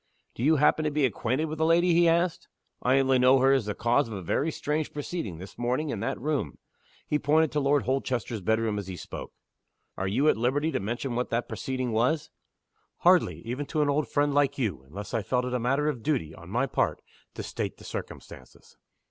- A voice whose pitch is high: No, low, 130 Hz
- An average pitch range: Yes, average, 4.6 semitones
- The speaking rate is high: Yes, fast, 220 wpm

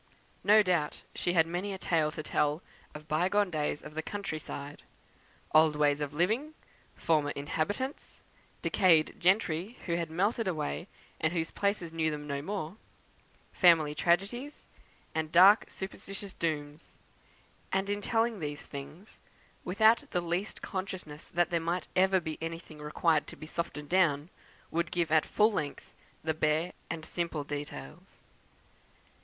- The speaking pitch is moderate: Yes, medium, 165 Hz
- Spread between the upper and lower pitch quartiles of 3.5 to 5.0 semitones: Yes, average, 3.9 semitones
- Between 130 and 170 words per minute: Yes, average, 150 wpm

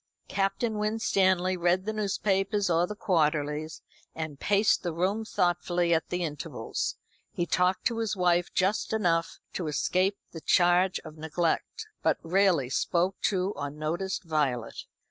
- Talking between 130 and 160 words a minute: Yes, average, 140 wpm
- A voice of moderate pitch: Yes, medium, 180 Hz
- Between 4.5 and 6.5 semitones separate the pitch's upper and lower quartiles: No, average, 3.2 semitones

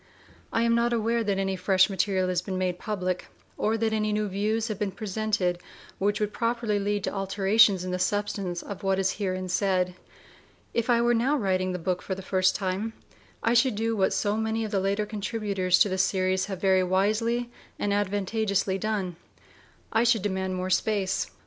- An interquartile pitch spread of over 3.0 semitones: No, average, 2.7 semitones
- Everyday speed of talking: Yes, average, 195 wpm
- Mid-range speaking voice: No, high, 200 Hz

